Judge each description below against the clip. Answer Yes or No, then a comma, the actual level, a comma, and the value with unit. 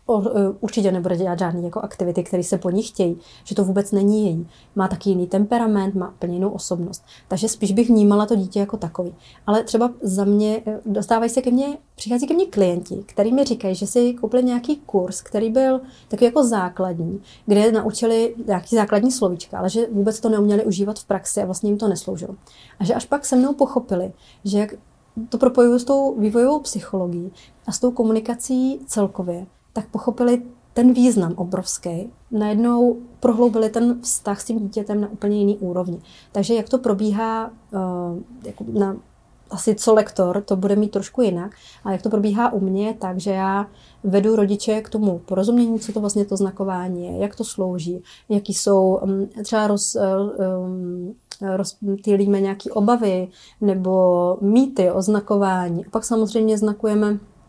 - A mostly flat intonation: No, average, 3.0 semitones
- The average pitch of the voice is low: No, high, 205 Hz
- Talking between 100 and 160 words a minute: No, fast, 170 wpm